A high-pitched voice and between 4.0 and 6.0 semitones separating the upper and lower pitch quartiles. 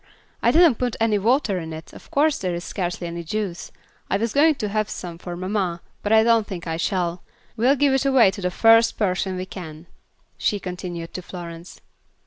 Yes: high, 195 Hz; average, 4.6 semitones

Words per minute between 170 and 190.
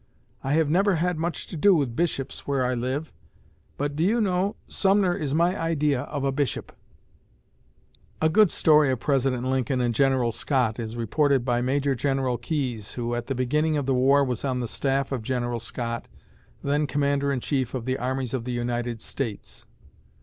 Yes: average, 185 wpm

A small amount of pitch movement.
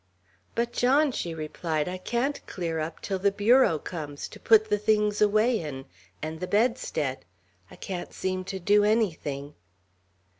No: wide, 5.4 semitones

